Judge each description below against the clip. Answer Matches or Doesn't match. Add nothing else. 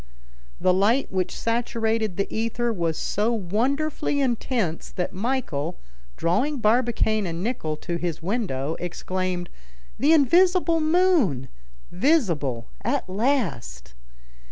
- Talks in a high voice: Matches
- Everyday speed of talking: Doesn't match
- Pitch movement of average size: Doesn't match